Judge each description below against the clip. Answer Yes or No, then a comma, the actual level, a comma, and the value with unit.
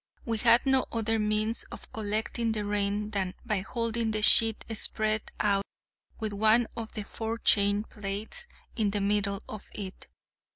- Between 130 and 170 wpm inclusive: Yes, average, 155 wpm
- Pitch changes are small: Yes, narrow, 1.7 semitones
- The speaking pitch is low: No, high, 215 Hz